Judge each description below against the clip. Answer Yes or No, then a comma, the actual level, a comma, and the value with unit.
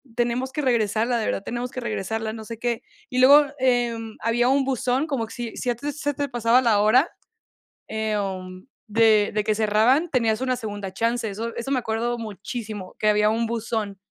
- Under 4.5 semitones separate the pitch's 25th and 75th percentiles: Yes, narrow, 2.6 semitones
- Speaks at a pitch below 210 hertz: No, high, 230 Hz